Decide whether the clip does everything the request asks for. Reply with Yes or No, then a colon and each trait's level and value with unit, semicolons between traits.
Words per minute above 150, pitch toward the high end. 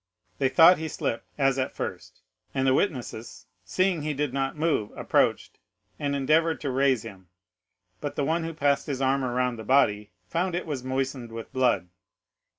No: average, 175 wpm; low, 135 Hz